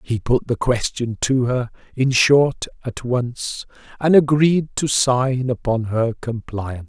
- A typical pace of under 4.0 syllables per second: Yes, 3.8 syllables/s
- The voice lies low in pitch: Yes, low, 125 Hz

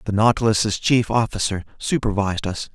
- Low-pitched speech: Yes, low, 105 Hz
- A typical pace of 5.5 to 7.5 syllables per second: No, 5.3 syllables/s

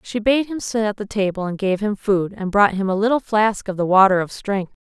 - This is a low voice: No, high, 205 Hz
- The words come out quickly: Yes, fast, 275 wpm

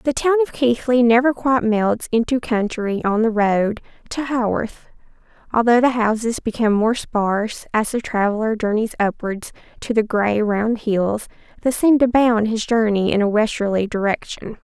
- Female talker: Yes, female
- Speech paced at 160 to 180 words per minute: Yes, average, 165 wpm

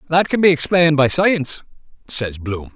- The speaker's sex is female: No, male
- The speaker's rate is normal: Yes, average, 175 wpm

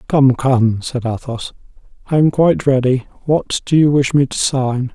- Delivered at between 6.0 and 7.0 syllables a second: No, 4.5 syllables/s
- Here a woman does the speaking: No, male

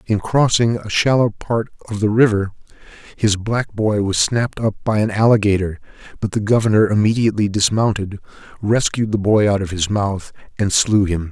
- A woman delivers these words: No, male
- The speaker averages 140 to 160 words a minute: No, average, 170 wpm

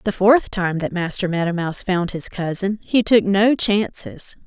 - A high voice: Yes, high, 195 Hz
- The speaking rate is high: No, average, 190 wpm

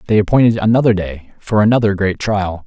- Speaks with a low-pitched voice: Yes, low, 100 Hz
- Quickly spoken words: No, average, 180 wpm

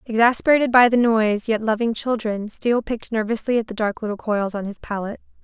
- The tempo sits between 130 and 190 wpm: No, average, 200 wpm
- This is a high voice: Yes, high, 225 Hz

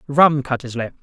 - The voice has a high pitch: No, low, 135 Hz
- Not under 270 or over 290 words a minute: No, fast, 235 wpm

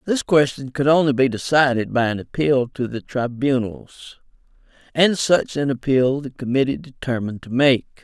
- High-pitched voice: No, low, 135 Hz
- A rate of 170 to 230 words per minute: No, average, 155 wpm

